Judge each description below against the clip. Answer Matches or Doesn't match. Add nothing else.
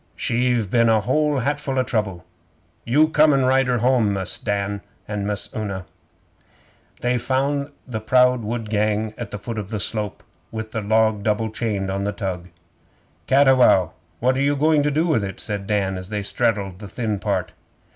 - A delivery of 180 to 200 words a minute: Matches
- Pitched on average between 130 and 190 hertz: Doesn't match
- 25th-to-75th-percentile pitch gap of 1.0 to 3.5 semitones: Doesn't match